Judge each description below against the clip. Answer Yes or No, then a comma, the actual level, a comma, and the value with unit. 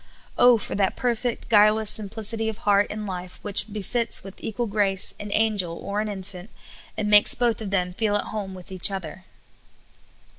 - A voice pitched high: Yes, high, 205 Hz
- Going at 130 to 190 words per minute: Yes, average, 180 wpm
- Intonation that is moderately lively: No, narrow, 2.2 semitones